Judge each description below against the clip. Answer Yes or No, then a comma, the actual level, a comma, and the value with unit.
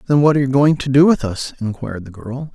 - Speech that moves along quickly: Yes, fast, 285 wpm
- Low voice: Yes, low, 130 Hz